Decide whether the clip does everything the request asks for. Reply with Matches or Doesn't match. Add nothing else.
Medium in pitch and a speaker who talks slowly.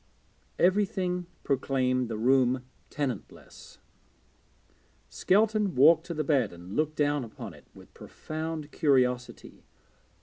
Matches